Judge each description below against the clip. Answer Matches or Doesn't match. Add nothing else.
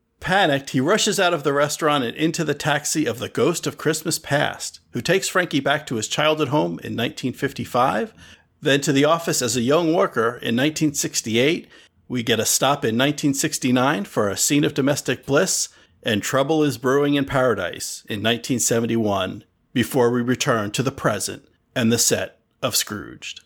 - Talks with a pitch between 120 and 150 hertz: Matches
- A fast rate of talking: Doesn't match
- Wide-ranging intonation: Doesn't match